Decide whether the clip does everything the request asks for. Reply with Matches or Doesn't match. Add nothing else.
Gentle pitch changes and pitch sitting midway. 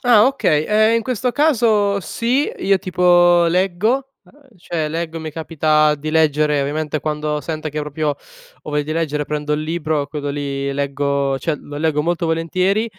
Doesn't match